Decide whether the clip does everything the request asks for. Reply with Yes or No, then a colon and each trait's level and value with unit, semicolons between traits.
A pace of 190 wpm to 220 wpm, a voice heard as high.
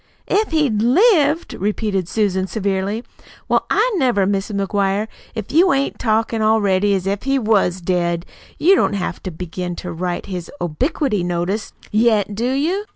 No: average, 155 wpm; high, 205 Hz